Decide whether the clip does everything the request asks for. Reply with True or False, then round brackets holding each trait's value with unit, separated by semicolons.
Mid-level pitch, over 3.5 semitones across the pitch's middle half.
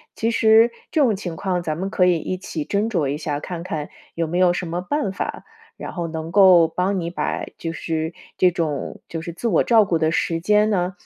False (175 Hz; 3.2 semitones)